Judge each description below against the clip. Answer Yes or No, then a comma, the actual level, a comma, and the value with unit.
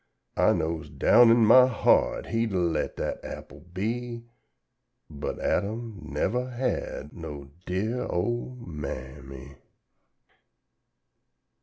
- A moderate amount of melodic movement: No, wide, 7.7 semitones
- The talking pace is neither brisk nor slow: No, slow, 115 wpm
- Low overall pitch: Yes, low, 100 Hz